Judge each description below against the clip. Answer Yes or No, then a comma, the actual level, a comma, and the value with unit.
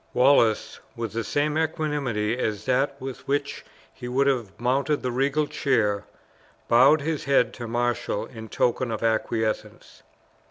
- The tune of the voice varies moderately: Yes, average, 3.5 semitones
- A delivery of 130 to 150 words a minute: Yes, average, 145 wpm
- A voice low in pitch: Yes, low, 125 Hz